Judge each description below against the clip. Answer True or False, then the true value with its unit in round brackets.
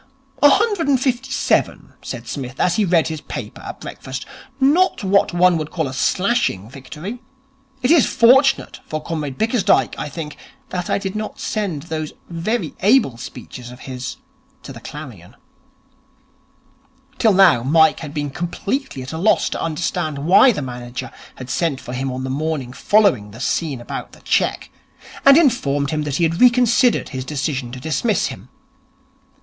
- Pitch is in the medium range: True (165 Hz)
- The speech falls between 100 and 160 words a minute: False (170 wpm)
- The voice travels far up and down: True (8.1 semitones)